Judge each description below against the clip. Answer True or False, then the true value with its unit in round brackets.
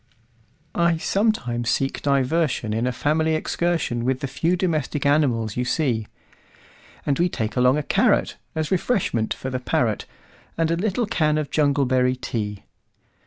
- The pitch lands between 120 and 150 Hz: True (140 Hz)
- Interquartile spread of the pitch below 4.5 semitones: False (4.8 semitones)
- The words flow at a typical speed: False (125 wpm)